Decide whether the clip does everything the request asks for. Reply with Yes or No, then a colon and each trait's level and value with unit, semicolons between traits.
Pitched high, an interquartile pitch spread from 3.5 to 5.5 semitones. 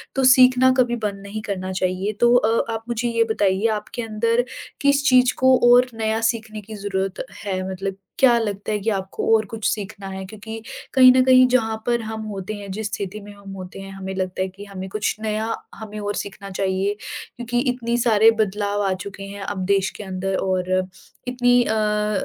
No: high, 210 Hz; average, 3.0 semitones